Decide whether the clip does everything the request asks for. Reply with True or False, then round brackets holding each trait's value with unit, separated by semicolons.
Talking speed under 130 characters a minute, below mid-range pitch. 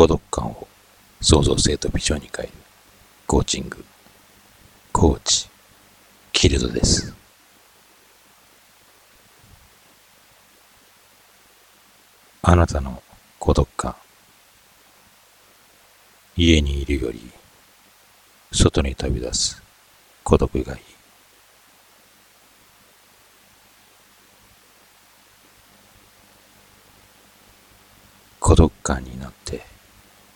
True (115 characters per minute; 95 Hz)